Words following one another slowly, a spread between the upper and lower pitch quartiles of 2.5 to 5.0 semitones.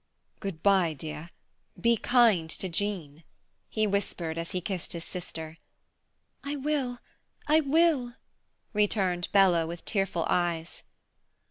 No: slow, 120 wpm; wide, 5.6 semitones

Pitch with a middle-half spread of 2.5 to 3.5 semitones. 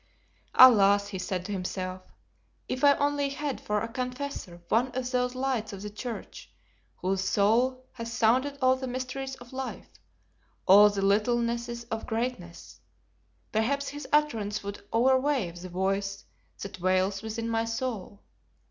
No: average, 4.4 semitones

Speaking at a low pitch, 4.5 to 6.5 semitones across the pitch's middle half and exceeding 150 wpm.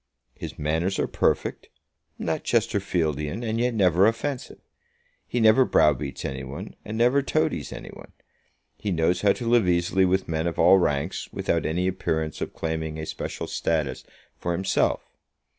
Yes: very low, 90 Hz; wide, 5.5 semitones; average, 160 wpm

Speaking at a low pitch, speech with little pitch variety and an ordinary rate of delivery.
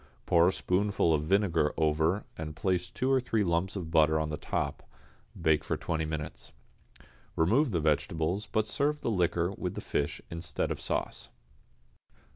No: very low, 85 Hz; average, 4.1 semitones; average, 165 wpm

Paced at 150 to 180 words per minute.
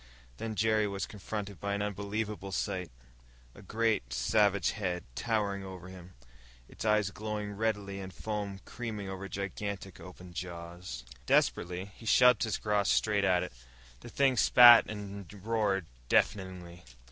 No: average, 140 wpm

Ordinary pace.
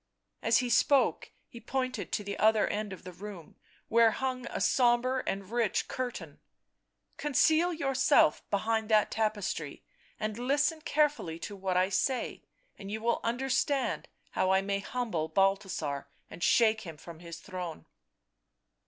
Yes: average, 155 wpm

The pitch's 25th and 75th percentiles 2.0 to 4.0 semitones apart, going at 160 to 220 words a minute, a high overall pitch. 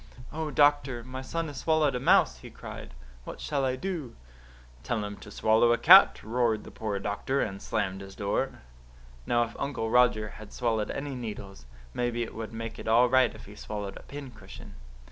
No: average, 3.7 semitones; average, 190 wpm; low, 120 Hz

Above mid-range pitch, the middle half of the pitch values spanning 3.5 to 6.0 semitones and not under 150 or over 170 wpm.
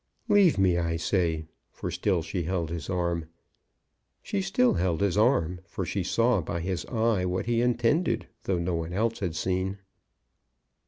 No: very low, 95 Hz; average, 4.6 semitones; average, 165 wpm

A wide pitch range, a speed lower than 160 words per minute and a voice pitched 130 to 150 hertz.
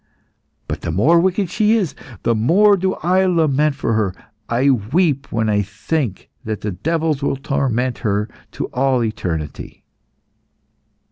Yes: wide, 7.6 semitones; average, 145 wpm; low, 135 Hz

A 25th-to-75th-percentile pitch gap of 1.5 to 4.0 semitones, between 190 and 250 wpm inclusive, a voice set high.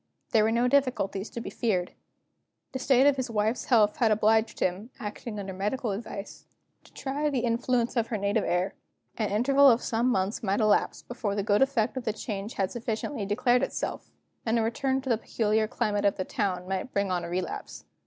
Yes: average, 3.3 semitones; fast, 205 wpm; high, 220 Hz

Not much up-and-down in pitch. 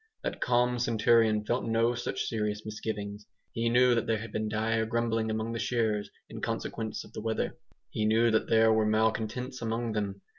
Yes: narrow, 1.3 semitones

